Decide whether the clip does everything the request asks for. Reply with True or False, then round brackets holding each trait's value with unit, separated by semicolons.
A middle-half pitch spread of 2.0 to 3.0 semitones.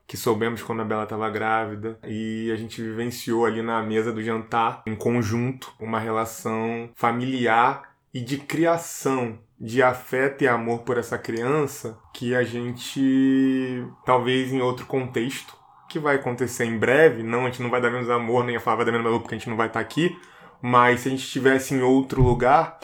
True (2.4 semitones)